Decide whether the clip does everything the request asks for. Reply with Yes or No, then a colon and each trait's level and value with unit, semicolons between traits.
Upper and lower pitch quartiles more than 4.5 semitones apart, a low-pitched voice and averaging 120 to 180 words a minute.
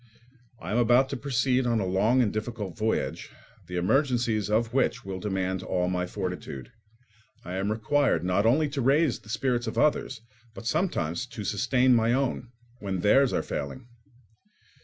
Yes: average, 5.1 semitones; low, 115 Hz; average, 165 wpm